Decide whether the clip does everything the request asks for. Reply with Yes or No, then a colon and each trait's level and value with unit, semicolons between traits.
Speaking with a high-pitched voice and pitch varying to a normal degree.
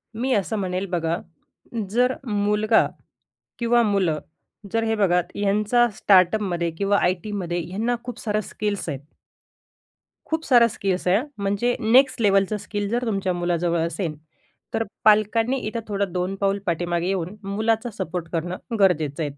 Yes: high, 200 Hz; average, 3.6 semitones